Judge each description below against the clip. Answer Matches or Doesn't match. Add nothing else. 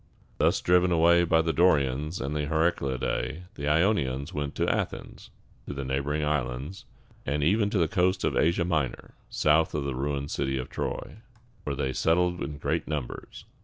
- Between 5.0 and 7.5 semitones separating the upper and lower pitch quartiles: Doesn't match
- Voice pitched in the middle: Doesn't match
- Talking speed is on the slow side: Doesn't match